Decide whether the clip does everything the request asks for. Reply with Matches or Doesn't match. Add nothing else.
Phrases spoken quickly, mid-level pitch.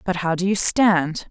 Matches